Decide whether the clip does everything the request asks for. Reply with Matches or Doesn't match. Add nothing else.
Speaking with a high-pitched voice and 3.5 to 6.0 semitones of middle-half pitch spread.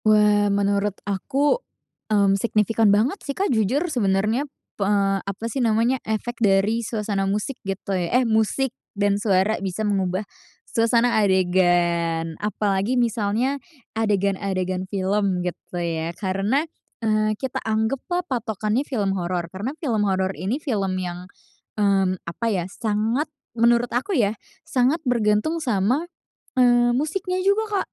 Matches